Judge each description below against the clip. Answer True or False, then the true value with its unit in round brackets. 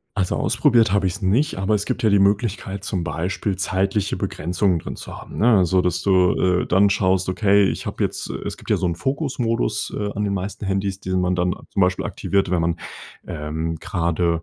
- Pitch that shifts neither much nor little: False (2.2 semitones)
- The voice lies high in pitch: False (95 Hz)